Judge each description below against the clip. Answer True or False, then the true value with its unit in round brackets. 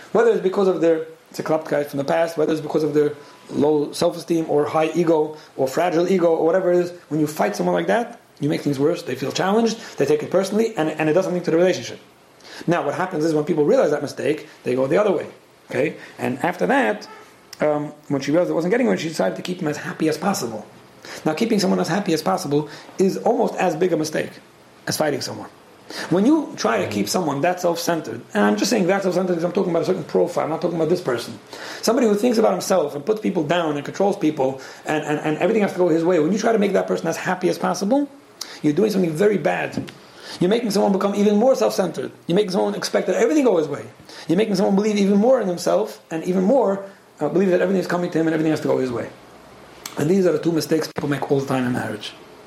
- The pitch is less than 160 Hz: False (175 Hz)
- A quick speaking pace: True (260 wpm)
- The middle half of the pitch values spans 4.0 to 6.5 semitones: True (4.3 semitones)